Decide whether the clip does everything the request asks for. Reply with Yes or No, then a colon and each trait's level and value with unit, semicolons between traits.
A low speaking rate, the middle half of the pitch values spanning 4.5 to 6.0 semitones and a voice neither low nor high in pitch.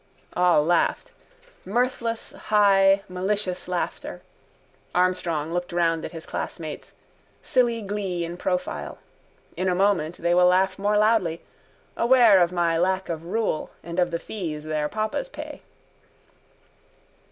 No: slow, 130 wpm; average, 3.3 semitones; medium, 180 Hz